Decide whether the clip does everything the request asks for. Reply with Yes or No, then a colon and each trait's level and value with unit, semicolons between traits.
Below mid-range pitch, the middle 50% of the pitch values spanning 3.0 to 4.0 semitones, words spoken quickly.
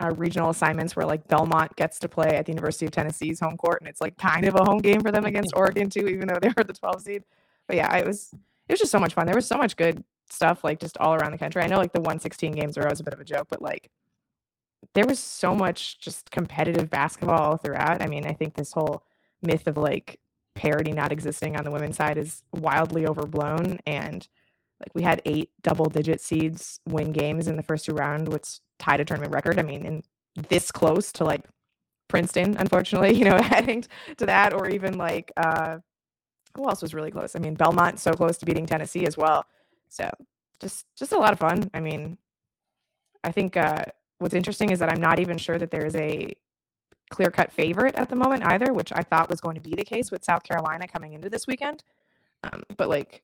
No: medium, 165 Hz; average, 3.4 semitones; fast, 225 wpm